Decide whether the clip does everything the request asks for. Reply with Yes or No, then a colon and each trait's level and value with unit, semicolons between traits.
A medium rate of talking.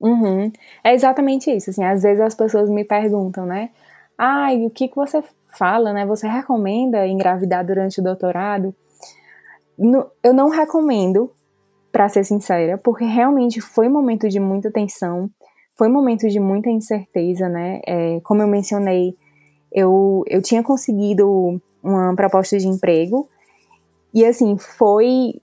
Yes: average, 150 wpm